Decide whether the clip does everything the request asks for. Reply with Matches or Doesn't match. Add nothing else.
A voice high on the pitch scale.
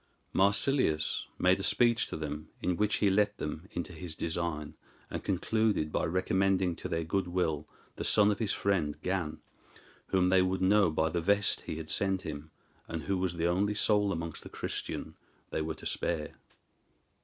Doesn't match